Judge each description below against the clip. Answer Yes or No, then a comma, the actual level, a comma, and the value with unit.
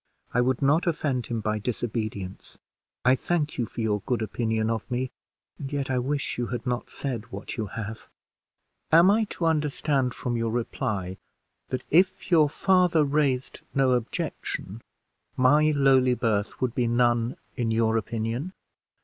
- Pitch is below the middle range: Yes, low, 125 Hz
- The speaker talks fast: No, average, 160 wpm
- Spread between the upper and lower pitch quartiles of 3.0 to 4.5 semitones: Yes, average, 4.0 semitones